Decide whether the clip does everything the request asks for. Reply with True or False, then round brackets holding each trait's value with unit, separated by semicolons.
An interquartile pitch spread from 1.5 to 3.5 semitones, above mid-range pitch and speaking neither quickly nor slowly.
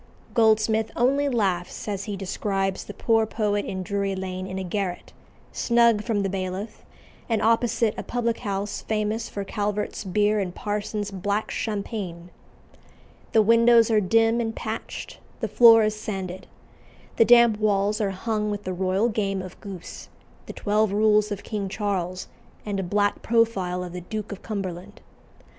True (2.4 semitones; 205 Hz; 160 wpm)